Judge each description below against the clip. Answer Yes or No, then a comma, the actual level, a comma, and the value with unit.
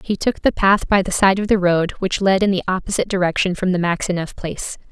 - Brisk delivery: Yes, fast, 245 wpm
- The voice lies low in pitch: No, high, 190 Hz